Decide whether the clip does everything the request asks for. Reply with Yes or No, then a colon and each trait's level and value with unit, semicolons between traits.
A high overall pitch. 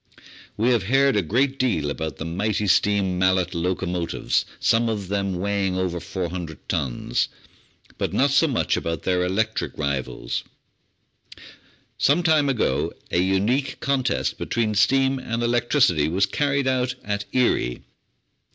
No: low, 100 Hz